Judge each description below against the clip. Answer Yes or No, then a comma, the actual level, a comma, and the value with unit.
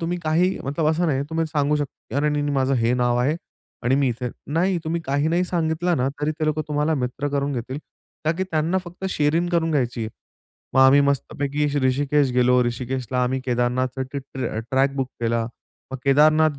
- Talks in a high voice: No, medium, 145 Hz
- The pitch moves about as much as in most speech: Yes, average, 3.4 semitones